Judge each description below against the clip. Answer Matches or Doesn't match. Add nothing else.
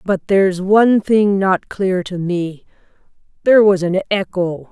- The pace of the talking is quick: Doesn't match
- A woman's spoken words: Matches